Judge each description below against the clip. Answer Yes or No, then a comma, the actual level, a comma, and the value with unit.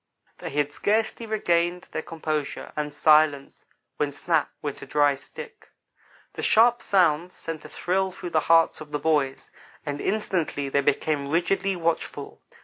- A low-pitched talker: No, medium, 160 Hz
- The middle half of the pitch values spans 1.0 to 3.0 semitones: No, average, 3.7 semitones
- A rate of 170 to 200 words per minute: No, average, 150 wpm